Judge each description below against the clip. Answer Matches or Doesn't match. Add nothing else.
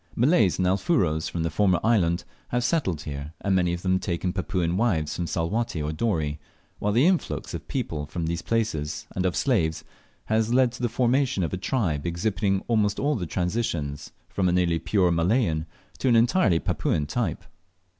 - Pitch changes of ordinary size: Doesn't match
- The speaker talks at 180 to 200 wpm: Matches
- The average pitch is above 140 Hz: Doesn't match